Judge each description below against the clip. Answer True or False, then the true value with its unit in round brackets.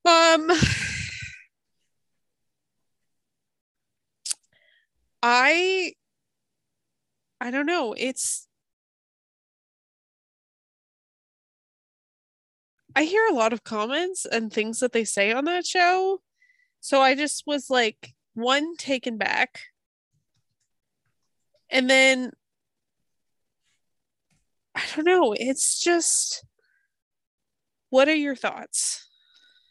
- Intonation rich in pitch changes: True (6.1 semitones)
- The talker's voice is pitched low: False (290 Hz)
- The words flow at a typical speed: False (80 wpm)